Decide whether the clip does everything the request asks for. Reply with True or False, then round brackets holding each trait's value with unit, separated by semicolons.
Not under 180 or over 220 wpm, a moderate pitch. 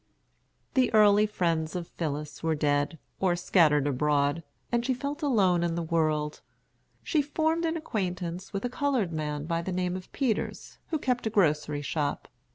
False (165 wpm; 175 Hz)